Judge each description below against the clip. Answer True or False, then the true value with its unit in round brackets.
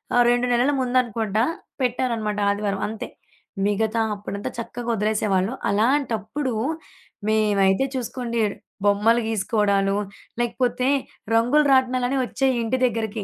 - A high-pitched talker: True (230 Hz)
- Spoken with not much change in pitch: False (3.0 semitones)